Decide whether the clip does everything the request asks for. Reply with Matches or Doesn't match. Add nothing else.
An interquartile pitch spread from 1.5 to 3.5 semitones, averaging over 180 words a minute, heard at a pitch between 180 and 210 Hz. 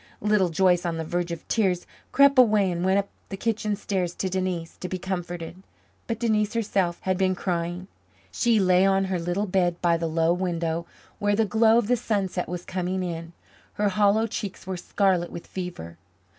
Matches